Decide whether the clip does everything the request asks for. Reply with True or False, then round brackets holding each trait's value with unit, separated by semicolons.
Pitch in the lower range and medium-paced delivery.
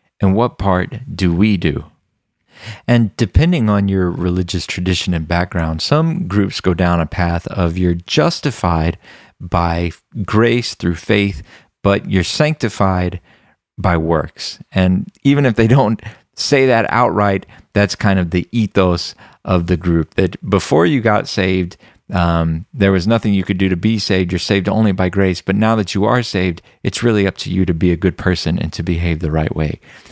True (95 Hz; 180 wpm)